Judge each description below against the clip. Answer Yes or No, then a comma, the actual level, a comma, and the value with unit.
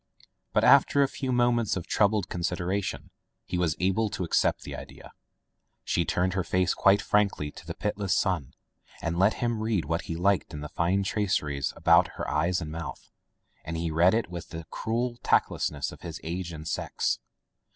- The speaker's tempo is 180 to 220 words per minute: Yes, average, 185 wpm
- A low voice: Yes, very low, 90 Hz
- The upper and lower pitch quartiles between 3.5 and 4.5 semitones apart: Yes, average, 3.8 semitones